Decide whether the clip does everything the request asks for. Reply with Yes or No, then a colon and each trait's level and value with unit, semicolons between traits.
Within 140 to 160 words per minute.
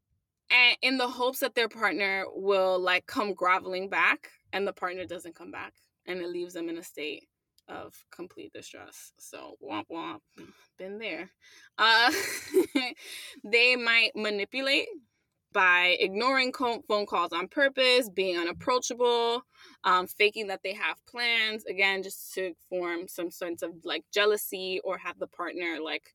Yes: average, 150 wpm